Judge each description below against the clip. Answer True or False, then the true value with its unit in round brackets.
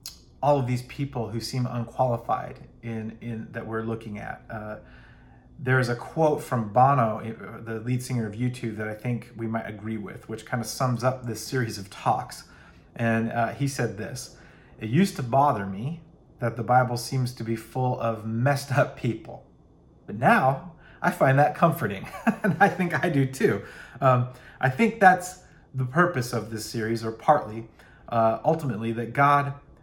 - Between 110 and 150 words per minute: False (180 wpm)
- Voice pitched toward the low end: True (125 Hz)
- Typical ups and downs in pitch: True (3.7 semitones)